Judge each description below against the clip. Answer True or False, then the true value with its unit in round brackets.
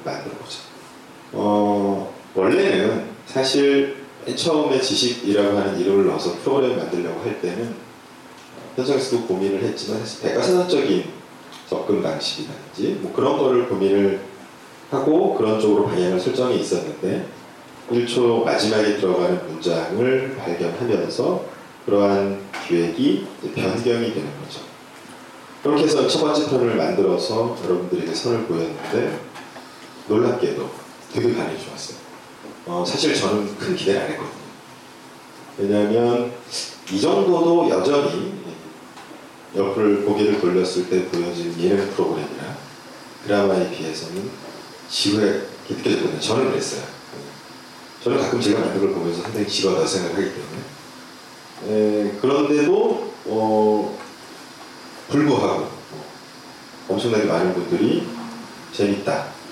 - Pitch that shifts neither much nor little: True (4.7 semitones)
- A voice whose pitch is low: True (105 Hz)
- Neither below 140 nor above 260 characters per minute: False (275 characters per minute)